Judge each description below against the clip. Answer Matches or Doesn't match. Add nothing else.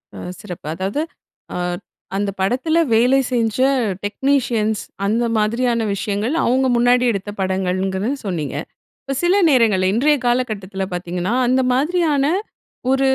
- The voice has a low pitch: Doesn't match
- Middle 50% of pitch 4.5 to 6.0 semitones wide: Matches